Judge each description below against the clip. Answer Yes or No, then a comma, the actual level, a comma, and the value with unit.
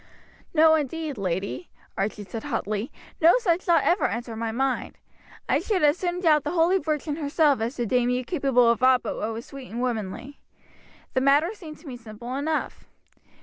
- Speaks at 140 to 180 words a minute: No, average, 190 wpm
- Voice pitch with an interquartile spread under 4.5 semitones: No, wide, 5.4 semitones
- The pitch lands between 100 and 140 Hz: No, very high, 270 Hz